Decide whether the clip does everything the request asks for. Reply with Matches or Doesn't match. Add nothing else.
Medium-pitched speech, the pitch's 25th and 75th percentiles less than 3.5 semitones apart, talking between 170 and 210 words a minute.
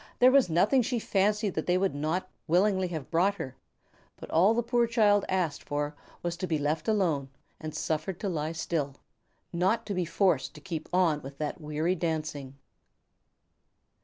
Doesn't match